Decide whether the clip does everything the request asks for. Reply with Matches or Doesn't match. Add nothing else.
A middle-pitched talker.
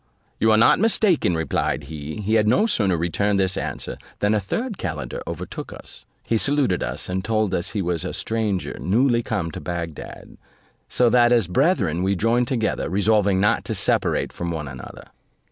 Doesn't match